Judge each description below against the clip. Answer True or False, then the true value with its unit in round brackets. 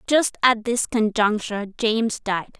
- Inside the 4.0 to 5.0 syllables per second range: True (4.5 syllables/s)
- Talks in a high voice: True (225 Hz)